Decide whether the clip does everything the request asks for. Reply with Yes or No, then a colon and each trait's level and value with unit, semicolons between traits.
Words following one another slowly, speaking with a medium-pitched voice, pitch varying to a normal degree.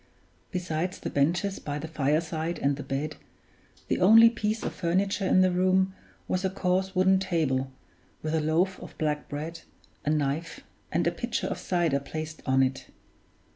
No: average, 170 wpm; medium, 165 Hz; average, 3.9 semitones